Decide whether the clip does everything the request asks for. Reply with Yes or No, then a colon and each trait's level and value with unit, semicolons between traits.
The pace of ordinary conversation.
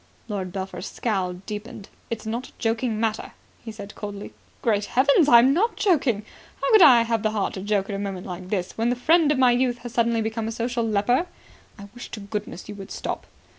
No: fast, 215 wpm